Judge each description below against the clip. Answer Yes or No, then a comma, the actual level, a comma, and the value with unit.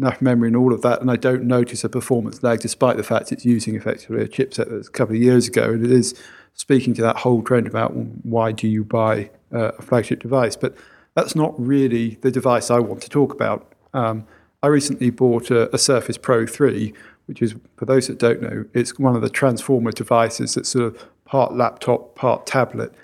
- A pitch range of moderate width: No, narrow, 2.1 semitones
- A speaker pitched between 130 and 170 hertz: No, low, 120 Hz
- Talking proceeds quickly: Yes, fast, 220 wpm